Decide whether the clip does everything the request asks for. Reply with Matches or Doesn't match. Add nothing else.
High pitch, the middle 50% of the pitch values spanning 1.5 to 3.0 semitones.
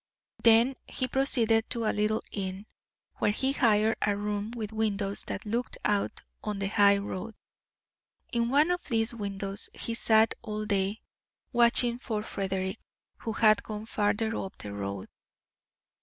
Matches